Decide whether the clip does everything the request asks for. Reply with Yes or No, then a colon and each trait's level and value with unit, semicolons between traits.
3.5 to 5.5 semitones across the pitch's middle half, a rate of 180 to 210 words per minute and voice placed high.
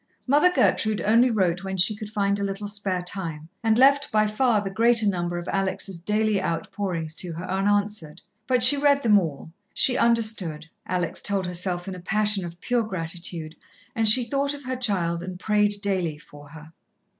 Yes: average, 4.0 semitones; average, 185 wpm; high, 200 Hz